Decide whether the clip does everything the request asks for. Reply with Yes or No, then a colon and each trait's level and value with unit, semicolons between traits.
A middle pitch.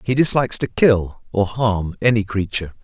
No: low, 105 Hz